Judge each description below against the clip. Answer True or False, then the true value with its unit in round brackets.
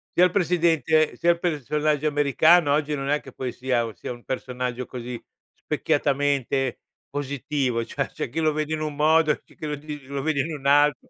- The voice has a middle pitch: True (145 Hz)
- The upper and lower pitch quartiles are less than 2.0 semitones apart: False (2.7 semitones)